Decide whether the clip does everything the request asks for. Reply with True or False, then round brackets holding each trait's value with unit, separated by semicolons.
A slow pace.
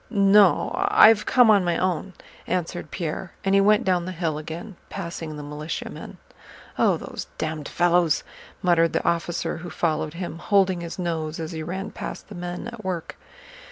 False (170 wpm)